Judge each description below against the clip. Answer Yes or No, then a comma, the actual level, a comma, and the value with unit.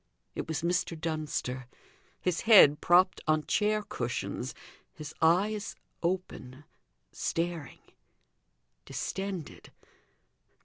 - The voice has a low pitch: No, medium, 170 Hz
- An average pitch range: Yes, average, 3.4 semitones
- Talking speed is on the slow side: Yes, slow, 85 wpm